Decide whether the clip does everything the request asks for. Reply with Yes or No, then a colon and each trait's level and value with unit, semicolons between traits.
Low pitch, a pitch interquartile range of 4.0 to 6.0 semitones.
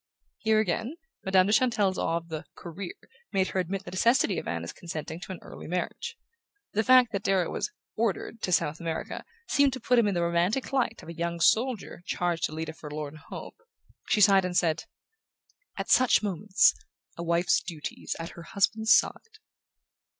No: medium, 185 Hz; average, 4.5 semitones